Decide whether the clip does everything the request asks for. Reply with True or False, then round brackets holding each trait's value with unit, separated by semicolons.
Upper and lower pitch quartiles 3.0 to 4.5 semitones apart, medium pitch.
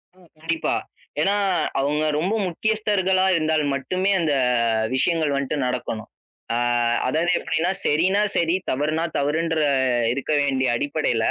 True (3.8 semitones; 160 Hz)